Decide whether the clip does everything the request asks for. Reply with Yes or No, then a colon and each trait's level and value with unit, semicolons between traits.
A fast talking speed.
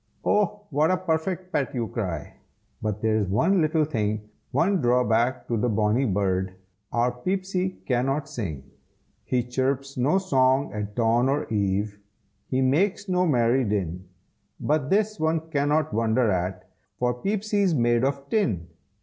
No: average, 145 wpm